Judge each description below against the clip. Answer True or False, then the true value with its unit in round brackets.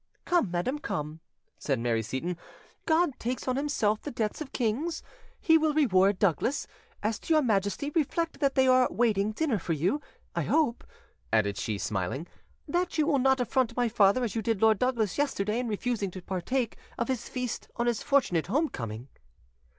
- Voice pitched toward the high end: True (235 Hz)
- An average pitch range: False (6.4 semitones)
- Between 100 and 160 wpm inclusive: False (180 wpm)